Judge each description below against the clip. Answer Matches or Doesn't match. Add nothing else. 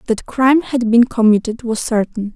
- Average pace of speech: Matches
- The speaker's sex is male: Doesn't match